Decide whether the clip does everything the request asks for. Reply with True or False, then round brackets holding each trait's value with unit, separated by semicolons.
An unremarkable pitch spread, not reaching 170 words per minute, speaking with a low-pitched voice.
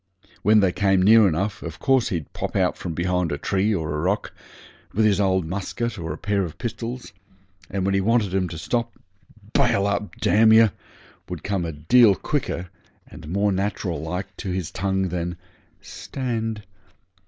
False (3.3 semitones; 175 wpm; 95 Hz)